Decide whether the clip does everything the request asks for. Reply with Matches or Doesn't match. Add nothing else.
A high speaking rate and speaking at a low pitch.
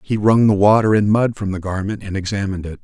Matches